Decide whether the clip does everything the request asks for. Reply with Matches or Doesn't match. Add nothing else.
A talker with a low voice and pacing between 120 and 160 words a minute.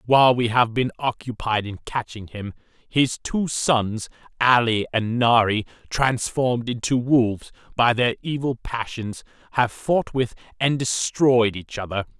Matches